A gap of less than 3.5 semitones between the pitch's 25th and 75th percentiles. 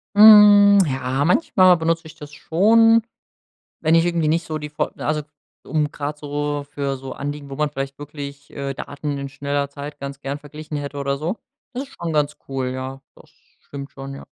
Yes: average, 2.7 semitones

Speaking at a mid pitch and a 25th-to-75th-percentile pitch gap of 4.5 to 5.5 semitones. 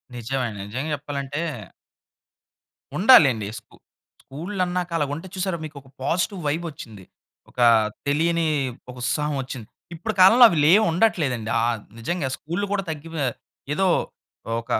Yes: medium, 155 Hz; average, 5.2 semitones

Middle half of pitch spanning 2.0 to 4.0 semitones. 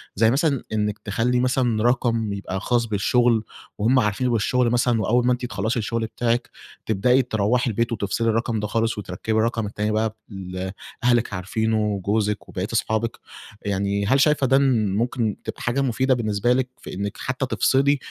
Yes: average, 2.8 semitones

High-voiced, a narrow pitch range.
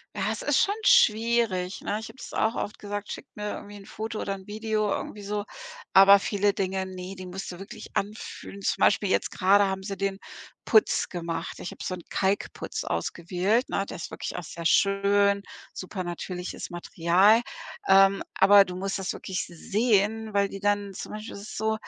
Yes: high, 200 Hz; narrow, 1.8 semitones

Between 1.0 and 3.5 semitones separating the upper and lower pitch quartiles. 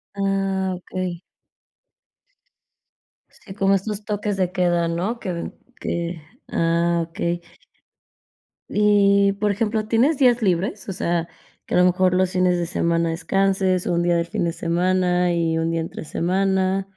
Yes: narrow, 2.5 semitones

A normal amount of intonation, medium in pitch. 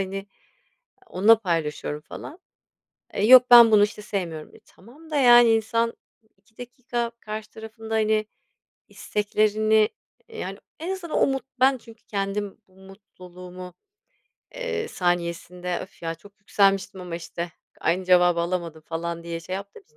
No: average, 4.3 semitones; high, 205 Hz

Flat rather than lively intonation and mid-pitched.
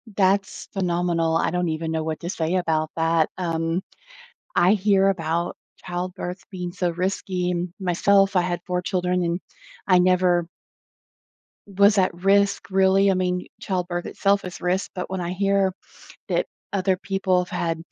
Yes: narrow, 1.8 semitones; medium, 180 Hz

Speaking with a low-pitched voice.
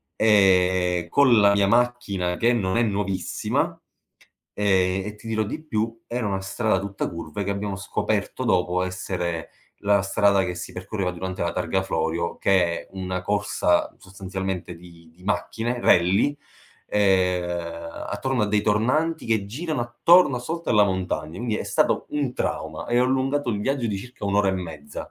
Yes: low, 100 Hz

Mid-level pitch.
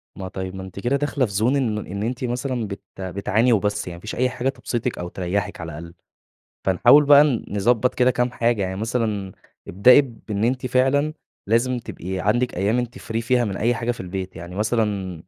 No: low, 110 Hz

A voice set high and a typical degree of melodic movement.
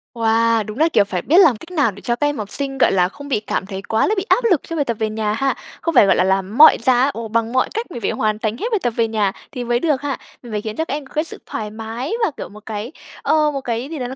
Yes: high, 235 Hz; average, 5.0 semitones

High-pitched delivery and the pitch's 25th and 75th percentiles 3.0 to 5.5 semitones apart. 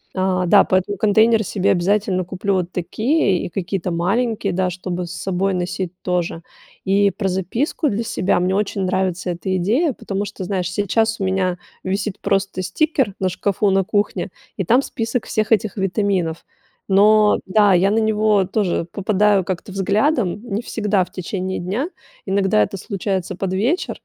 No: high, 195 Hz; narrow, 2.4 semitones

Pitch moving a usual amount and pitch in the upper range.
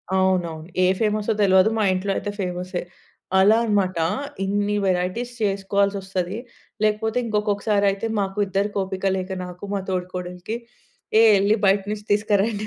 No: narrow, 2.0 semitones; high, 200 Hz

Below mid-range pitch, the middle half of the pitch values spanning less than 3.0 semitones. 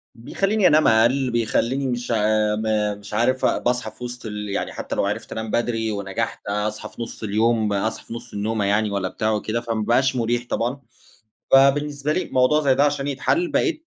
No: low, 115 Hz; average, 3.6 semitones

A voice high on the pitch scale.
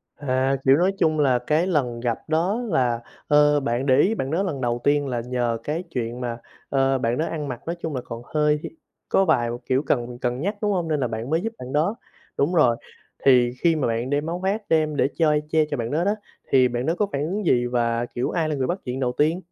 No: medium, 140 Hz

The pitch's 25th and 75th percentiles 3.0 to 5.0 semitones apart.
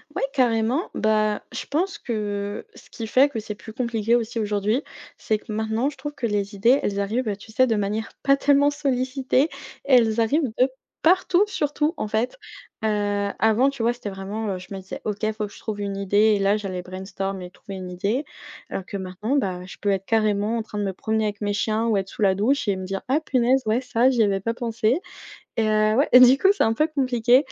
Yes: average, 3.9 semitones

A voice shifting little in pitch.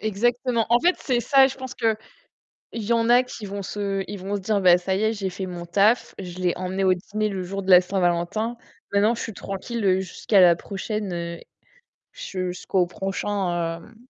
No: average, 3.4 semitones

